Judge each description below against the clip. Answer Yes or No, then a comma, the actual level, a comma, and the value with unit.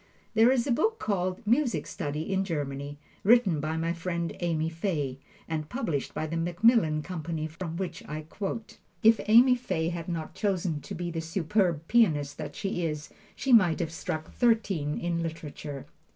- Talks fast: No, average, 170 wpm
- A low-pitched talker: No, medium, 170 Hz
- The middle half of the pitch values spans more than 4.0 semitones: Yes, average, 4.6 semitones